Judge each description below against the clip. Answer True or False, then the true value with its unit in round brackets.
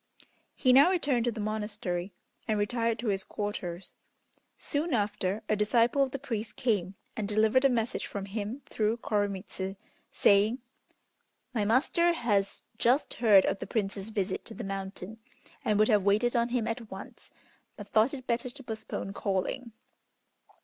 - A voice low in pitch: False (215 Hz)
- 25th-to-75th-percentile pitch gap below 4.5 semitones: True (3.1 semitones)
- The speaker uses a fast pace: False (160 wpm)